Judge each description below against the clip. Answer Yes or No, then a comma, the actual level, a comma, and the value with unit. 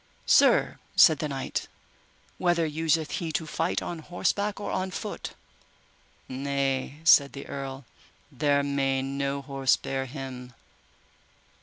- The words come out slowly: Yes, slow, 125 wpm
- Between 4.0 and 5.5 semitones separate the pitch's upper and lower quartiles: No, average, 2.9 semitones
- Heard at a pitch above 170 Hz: No, medium, 140 Hz